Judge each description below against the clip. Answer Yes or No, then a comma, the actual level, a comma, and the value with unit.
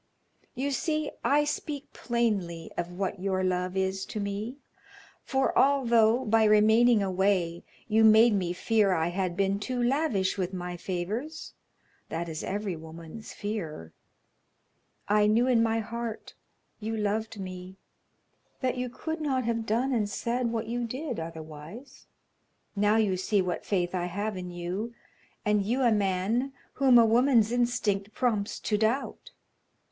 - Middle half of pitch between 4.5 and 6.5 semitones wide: No, average, 4.1 semitones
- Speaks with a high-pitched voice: Yes, high, 210 Hz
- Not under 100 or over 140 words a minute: No, average, 150 wpm